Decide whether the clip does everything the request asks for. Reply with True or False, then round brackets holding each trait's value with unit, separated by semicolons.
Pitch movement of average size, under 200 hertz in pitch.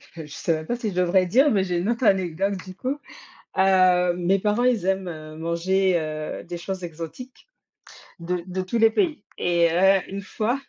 True (3.1 semitones; 185 Hz)